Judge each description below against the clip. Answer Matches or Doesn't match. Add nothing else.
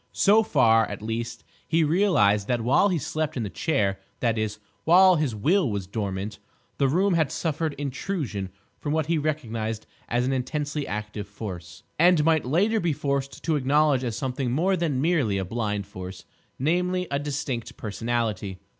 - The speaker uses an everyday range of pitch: Doesn't match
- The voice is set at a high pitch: Doesn't match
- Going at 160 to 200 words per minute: Matches